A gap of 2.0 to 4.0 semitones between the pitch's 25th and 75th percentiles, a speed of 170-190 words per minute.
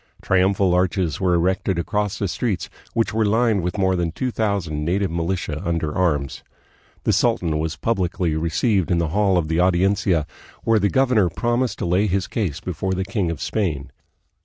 Yes: average, 3.4 semitones; average, 185 wpm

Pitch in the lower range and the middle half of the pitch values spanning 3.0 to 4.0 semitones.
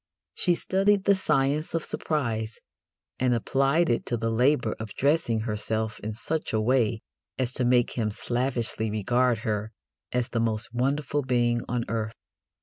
Yes: low, 120 Hz; average, 3.6 semitones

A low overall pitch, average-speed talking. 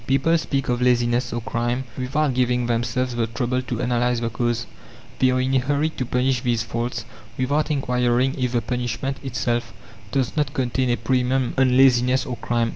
Yes: low, 125 Hz; average, 185 wpm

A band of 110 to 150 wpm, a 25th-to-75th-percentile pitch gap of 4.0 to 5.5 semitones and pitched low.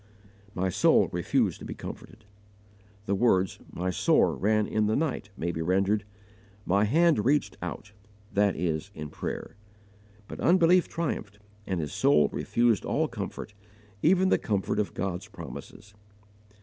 Yes: average, 145 wpm; average, 4.5 semitones; low, 105 Hz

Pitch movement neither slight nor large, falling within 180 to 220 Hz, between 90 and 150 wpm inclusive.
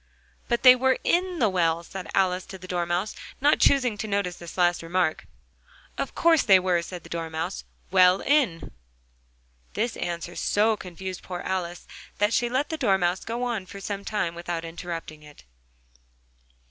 No: average, 4.4 semitones; medium, 185 Hz; average, 165 wpm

